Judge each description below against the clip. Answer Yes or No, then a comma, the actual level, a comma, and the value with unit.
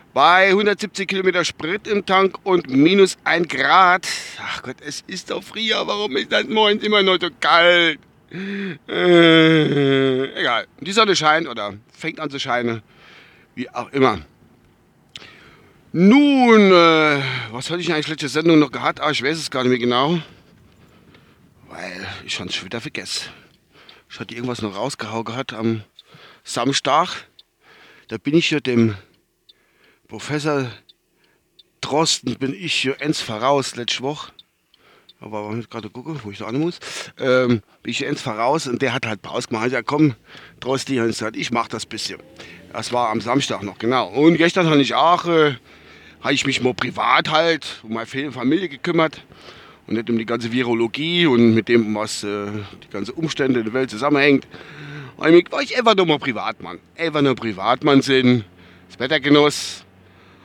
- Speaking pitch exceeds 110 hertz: Yes, medium, 140 Hz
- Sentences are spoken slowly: No, average, 165 wpm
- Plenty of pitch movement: Yes, wide, 5.8 semitones